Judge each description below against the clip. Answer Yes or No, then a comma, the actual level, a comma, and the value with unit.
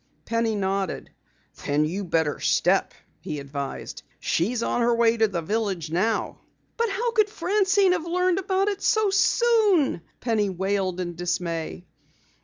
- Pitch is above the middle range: Yes, high, 225 Hz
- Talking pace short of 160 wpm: Yes, average, 145 wpm